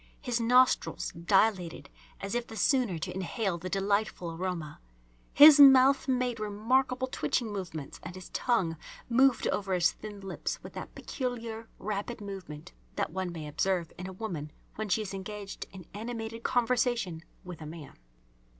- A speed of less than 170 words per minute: Yes, average, 155 wpm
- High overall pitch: Yes, high, 205 Hz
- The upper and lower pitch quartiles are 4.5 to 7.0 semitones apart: Yes, average, 4.9 semitones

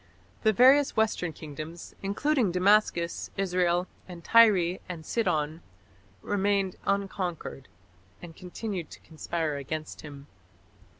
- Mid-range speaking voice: Yes, medium, 180 Hz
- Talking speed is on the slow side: Yes, slow, 105 wpm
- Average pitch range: Yes, average, 3.7 semitones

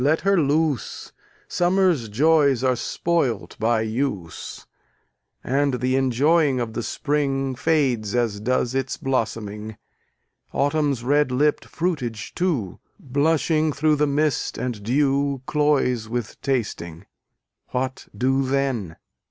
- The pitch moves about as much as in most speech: Yes, average, 3.9 semitones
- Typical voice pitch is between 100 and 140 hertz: Yes, low, 135 Hz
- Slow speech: Yes, slow, 115 wpm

